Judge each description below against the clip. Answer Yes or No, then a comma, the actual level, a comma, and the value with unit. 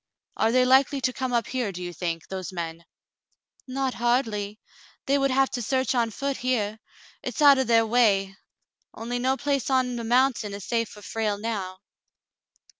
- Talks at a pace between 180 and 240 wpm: Yes, average, 185 wpm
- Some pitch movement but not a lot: Yes, average, 4.2 semitones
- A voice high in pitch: Yes, high, 235 Hz